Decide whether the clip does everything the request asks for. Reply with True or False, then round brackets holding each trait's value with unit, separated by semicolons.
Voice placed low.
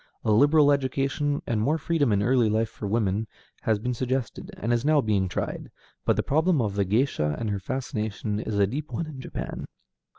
True (120 Hz)